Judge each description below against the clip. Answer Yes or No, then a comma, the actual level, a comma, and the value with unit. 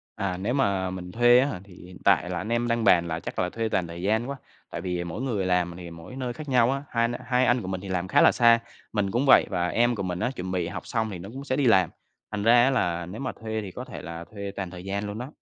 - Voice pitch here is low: Yes, low, 100 Hz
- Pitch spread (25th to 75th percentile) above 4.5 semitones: Yes, average, 5.1 semitones